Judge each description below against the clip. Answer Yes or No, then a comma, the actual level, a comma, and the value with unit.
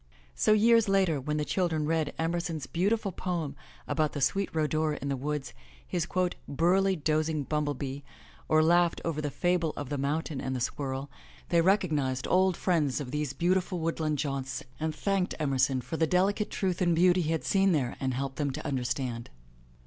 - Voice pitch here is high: No, medium, 155 Hz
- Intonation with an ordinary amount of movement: Yes, average, 4.0 semitones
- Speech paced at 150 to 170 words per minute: No, average, 180 wpm